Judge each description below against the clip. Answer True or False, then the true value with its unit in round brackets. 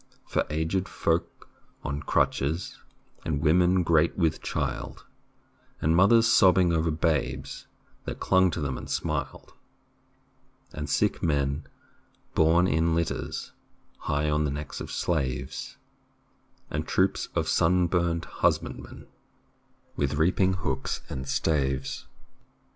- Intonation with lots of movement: False (3.3 semitones)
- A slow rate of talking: True (115 wpm)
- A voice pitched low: True (80 Hz)